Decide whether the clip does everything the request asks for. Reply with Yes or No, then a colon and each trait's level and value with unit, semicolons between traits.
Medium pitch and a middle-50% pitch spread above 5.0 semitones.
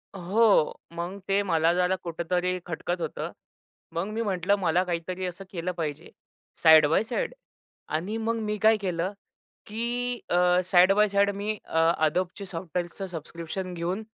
No: medium, 180 Hz; average, 3.0 semitones